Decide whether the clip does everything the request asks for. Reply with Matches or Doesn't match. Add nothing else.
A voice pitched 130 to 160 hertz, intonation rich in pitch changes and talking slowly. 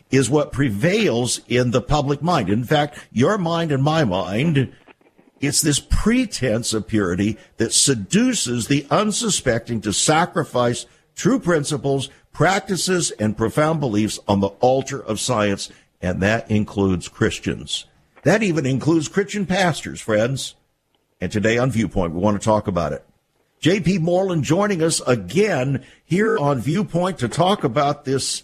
Doesn't match